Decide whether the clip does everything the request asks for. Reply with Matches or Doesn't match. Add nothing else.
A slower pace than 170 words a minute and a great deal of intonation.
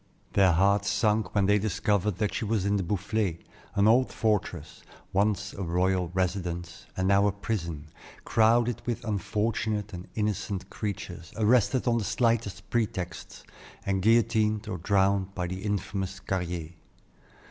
Doesn't match